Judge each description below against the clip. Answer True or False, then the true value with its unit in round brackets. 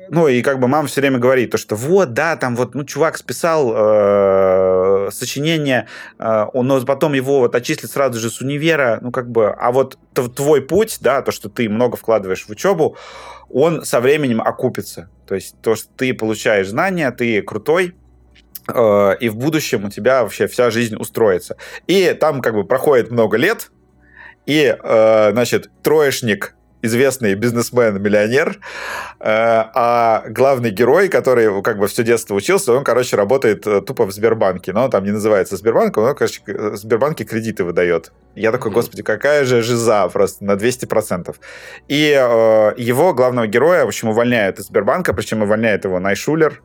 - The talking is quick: True (165 wpm)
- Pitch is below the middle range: True (120 Hz)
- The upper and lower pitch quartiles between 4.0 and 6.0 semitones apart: True (4.3 semitones)